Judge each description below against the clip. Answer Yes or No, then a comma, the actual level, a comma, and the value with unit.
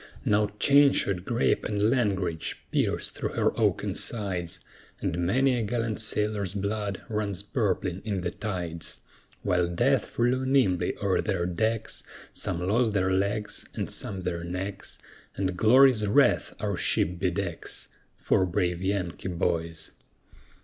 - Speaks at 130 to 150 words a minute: Yes, average, 140 wpm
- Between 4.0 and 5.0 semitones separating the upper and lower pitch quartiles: No, average, 3.3 semitones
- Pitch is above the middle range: No, low, 100 Hz